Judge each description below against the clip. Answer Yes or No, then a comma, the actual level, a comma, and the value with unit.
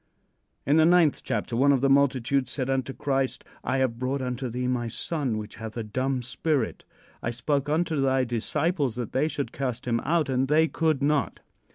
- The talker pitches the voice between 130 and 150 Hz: Yes, low, 135 Hz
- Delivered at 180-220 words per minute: Yes, average, 195 wpm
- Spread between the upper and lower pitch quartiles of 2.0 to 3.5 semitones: Yes, average, 2.7 semitones